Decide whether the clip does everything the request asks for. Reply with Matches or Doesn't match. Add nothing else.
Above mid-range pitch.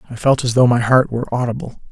Doesn't match